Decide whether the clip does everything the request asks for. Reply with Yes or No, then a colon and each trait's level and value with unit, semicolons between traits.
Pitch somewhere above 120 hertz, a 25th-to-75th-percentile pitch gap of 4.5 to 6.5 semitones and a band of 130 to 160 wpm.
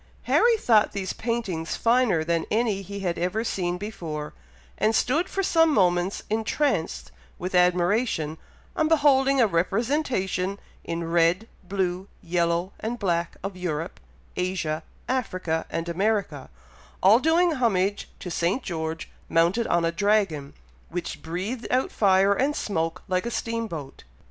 Yes: high, 190 Hz; average, 5.2 semitones; average, 140 wpm